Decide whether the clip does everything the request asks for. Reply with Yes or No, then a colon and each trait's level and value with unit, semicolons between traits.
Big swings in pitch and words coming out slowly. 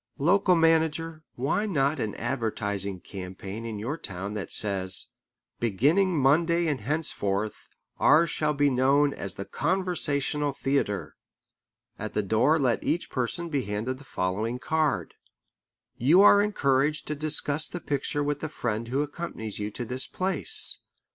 No: wide, 6.4 semitones; average, 145 wpm